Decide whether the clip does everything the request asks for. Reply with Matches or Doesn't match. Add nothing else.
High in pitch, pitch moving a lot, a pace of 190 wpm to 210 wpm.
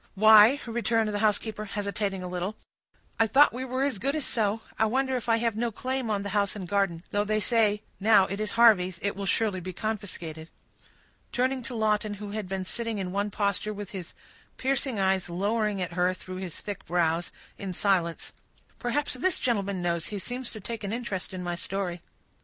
Doesn't match